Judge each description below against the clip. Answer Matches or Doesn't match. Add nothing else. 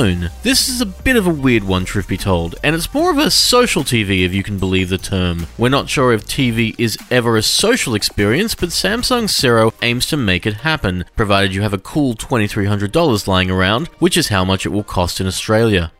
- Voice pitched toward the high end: Doesn't match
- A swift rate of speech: Matches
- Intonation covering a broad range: Matches